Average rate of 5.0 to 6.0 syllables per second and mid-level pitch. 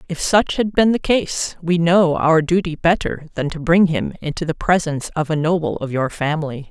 Yes: 5.1 syllables/s; medium, 165 Hz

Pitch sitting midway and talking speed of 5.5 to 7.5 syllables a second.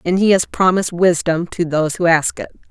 Yes: medium, 175 Hz; 5.7 syllables/s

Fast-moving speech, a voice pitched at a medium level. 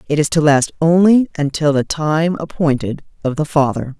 No: average, 180 wpm; medium, 155 Hz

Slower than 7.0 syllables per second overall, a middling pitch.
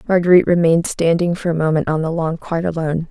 No: 7.2 syllables/s; medium, 165 Hz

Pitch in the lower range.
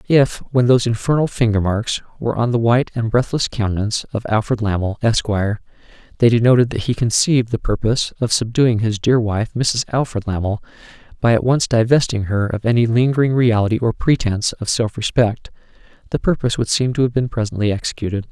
Yes: low, 115 Hz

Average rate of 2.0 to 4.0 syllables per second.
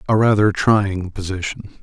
No: 4.7 syllables/s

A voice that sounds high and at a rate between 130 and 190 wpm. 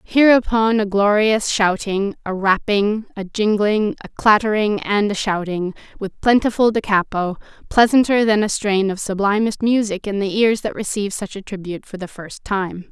Yes: high, 205 Hz; average, 165 wpm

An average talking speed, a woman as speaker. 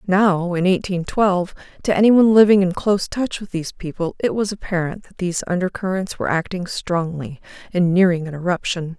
Yes: average, 175 wpm; female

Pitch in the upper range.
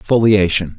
No: low, 100 Hz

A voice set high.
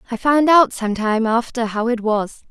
Yes: high, 235 Hz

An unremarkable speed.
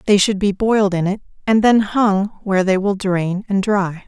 No: fast, 220 wpm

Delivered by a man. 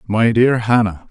Yes: male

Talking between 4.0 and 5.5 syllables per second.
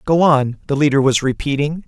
Yes: 5.4 syllables/s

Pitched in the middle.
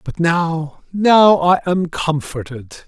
Yes: medium, 165 Hz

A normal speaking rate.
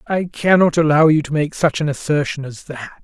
No: fast, 220 wpm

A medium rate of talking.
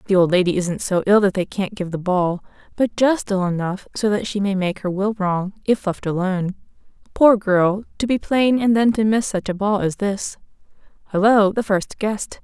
No: fast, 210 wpm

